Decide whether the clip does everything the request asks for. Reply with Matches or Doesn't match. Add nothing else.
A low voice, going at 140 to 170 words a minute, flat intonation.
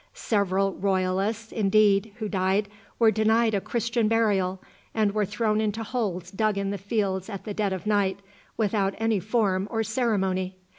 Doesn't match